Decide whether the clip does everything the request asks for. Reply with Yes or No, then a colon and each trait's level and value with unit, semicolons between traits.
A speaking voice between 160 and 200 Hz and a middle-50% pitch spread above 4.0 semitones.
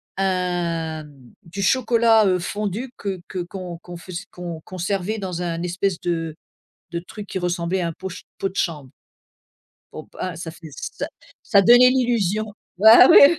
No: medium, 185 Hz; average, 3.3 semitones